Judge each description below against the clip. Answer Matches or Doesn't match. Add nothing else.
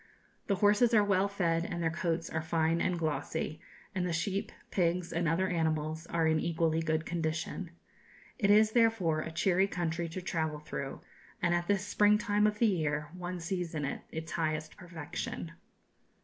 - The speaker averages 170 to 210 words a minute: Matches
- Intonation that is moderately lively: Matches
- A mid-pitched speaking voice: Matches